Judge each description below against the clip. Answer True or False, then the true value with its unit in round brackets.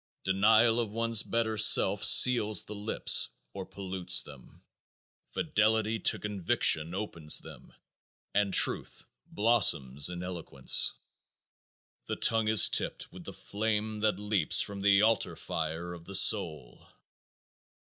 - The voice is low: True (105 Hz)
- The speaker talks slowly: True (125 wpm)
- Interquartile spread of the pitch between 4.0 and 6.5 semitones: False (3.5 semitones)